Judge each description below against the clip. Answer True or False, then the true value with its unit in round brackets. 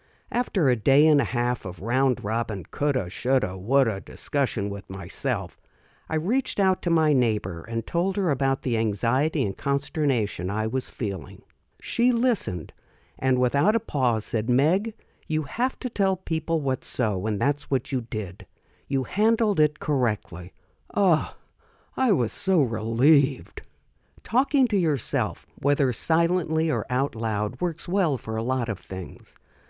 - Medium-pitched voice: False (130 Hz)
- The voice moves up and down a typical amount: False (6.7 semitones)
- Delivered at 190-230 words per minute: False (155 wpm)